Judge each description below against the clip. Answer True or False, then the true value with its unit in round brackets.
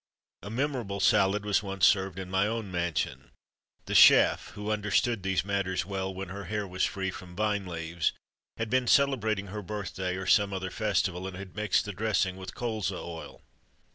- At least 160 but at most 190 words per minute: True (180 wpm)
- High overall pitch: False (100 Hz)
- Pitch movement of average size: False (2.3 semitones)